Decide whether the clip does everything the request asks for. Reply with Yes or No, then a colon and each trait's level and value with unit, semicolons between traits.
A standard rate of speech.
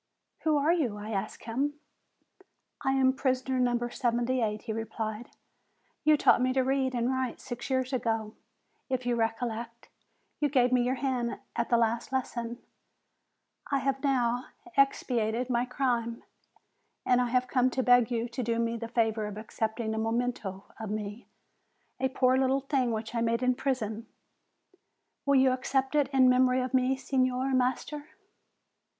Yes: average, 160 wpm